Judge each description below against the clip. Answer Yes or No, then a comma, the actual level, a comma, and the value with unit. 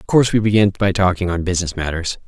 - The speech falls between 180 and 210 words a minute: No, fast, 235 wpm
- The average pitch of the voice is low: Yes, very low, 95 Hz